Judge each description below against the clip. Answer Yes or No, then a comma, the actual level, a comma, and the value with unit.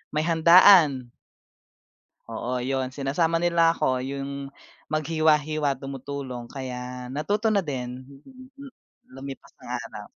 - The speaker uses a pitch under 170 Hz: Yes, medium, 140 Hz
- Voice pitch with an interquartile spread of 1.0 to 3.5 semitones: No, average, 4.1 semitones